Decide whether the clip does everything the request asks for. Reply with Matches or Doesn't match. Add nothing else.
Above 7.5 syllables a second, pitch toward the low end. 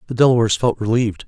Matches